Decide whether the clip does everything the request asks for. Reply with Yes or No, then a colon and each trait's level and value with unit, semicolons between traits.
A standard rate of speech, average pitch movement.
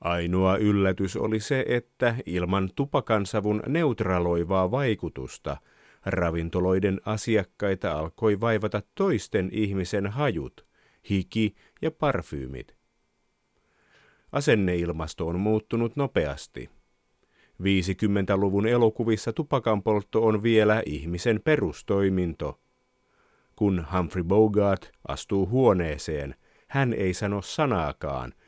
No: slow, 85 wpm; average, 3.6 semitones